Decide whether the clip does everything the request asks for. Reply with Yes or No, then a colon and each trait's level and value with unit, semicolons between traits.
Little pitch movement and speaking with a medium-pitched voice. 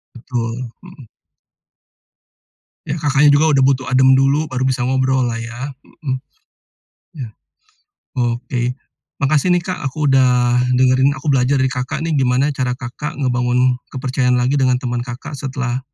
No: narrow, 2.0 semitones; low, 130 Hz